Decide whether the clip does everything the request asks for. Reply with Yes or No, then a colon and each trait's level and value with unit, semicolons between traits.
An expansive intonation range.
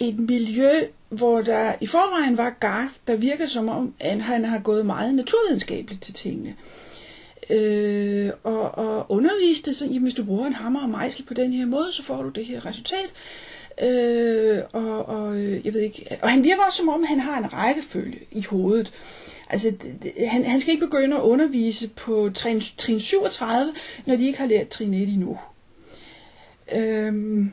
No: average, 3.8 semitones